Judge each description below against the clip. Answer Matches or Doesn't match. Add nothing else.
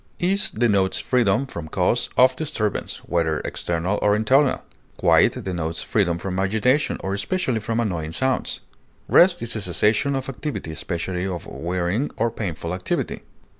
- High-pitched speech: Doesn't match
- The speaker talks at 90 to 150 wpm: Matches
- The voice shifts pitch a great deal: Matches